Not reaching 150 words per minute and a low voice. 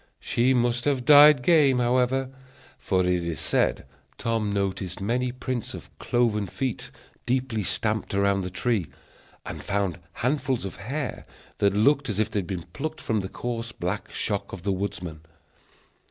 No: average, 160 wpm; low, 115 Hz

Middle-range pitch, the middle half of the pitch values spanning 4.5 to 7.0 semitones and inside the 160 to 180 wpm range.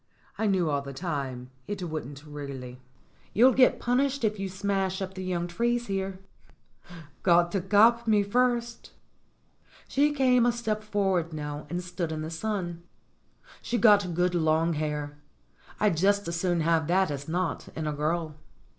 Yes: medium, 180 Hz; average, 5.0 semitones; average, 165 wpm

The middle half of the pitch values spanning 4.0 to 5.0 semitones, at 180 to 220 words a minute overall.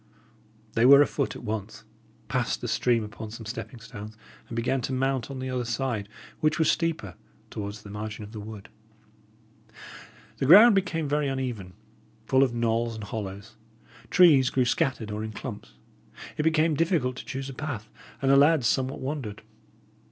No: average, 4.3 semitones; average, 170 wpm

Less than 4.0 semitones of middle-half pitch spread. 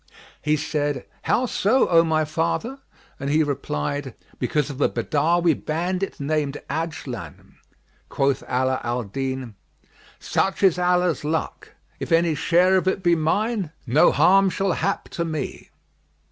No: average, 4.3 semitones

